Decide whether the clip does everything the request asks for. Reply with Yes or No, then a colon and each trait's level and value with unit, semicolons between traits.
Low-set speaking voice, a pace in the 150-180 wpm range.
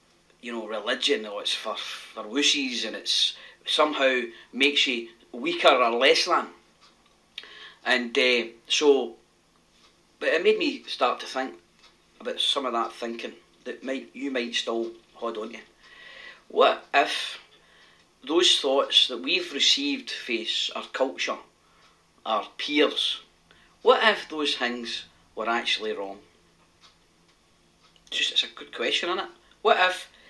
No: low, 125 Hz; slow, 135 wpm